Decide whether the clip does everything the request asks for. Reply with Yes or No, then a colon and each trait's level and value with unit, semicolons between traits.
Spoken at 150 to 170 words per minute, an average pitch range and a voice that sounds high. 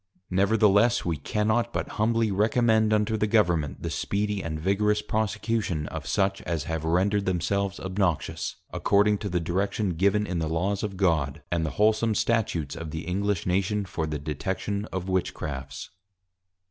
No: average, 160 wpm; average, 4.2 semitones; very low, 95 Hz